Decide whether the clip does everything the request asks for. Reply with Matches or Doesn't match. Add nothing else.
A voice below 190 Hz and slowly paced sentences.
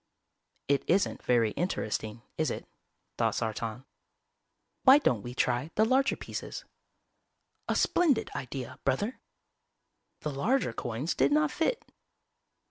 Matches